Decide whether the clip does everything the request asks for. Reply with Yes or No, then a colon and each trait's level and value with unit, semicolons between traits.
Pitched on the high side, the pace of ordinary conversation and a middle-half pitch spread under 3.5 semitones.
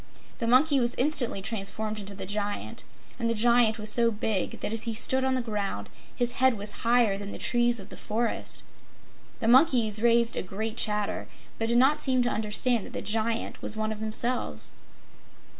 Yes: high, 225 Hz; average, 190 wpm; narrow, 2.5 semitones